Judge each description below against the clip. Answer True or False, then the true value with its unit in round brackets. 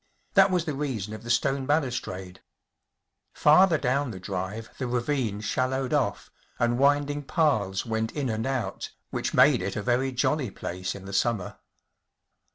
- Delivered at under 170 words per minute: True (160 wpm)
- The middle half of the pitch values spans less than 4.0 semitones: False (5.4 semitones)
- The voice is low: True (120 Hz)